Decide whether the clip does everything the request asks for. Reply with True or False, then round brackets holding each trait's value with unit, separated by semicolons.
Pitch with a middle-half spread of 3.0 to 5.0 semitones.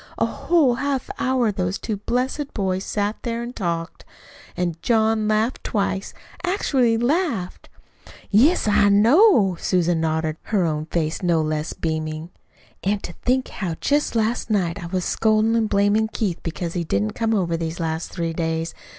False (5.5 semitones)